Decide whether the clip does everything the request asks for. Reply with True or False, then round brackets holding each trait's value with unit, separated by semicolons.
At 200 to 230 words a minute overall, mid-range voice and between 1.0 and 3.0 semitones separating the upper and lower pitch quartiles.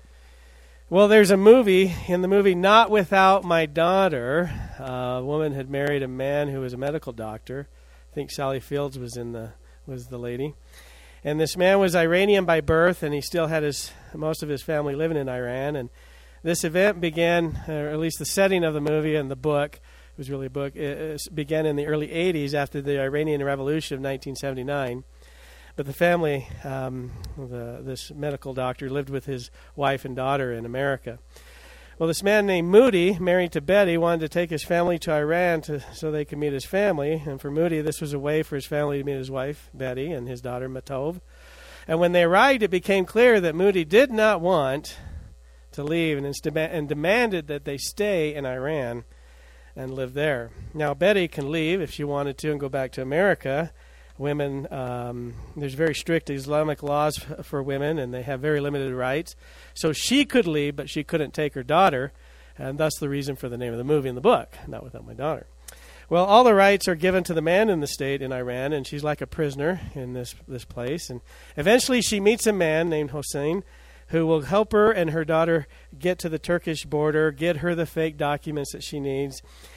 False (205 wpm; 150 Hz; 4.0 semitones)